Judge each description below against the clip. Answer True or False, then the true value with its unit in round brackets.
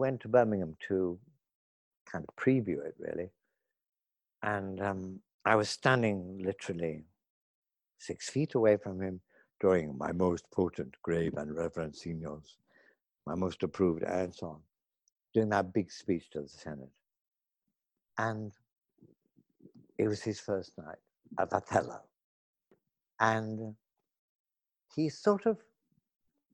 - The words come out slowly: True (120 wpm)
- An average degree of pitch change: True (4.4 semitones)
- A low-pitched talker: True (100 Hz)